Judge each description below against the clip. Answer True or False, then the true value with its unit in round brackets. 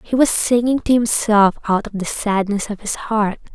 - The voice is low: False (215 Hz)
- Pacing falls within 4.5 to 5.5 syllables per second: True (4.6 syllables/s)